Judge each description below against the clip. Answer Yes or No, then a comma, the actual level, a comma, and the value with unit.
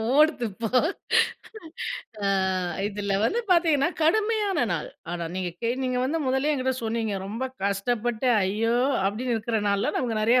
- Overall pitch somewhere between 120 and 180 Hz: No, high, 235 Hz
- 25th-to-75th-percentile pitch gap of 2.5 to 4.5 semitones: No, wide, 5.4 semitones